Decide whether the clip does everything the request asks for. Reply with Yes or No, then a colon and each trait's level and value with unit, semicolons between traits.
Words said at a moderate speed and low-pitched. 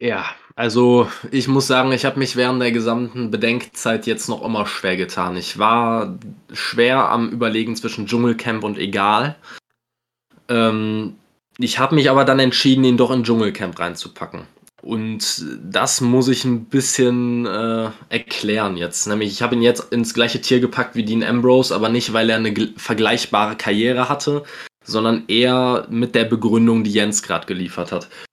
Yes: average, 160 wpm; low, 120 Hz